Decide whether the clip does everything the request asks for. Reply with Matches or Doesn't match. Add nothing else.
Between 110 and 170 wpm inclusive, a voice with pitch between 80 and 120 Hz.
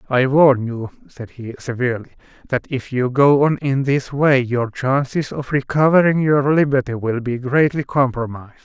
Doesn't match